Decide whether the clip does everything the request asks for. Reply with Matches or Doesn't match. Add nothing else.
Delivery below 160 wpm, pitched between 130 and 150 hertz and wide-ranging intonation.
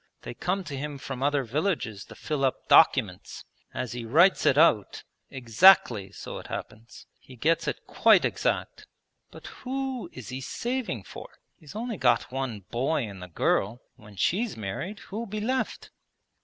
Doesn't match